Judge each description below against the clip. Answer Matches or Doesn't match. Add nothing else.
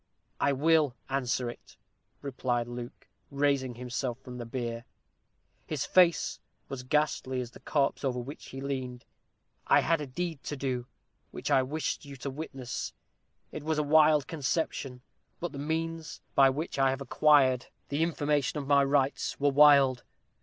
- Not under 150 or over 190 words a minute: Matches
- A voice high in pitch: Doesn't match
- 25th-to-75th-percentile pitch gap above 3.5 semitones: Doesn't match